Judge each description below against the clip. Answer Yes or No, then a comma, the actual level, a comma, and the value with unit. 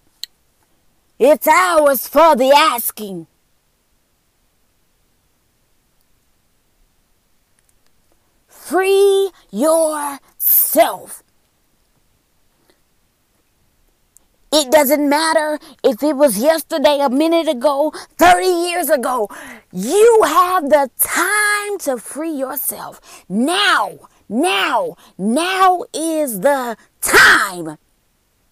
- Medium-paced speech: No, slow, 70 wpm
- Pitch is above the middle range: Yes, very high, 305 Hz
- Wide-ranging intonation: No, average, 3.6 semitones